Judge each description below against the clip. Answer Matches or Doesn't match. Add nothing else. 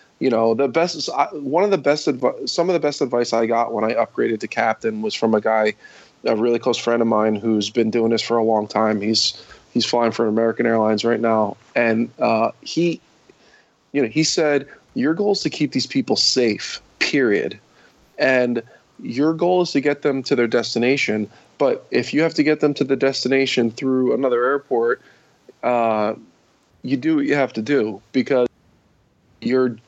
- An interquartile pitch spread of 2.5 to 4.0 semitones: Doesn't match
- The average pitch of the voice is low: Matches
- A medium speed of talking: Matches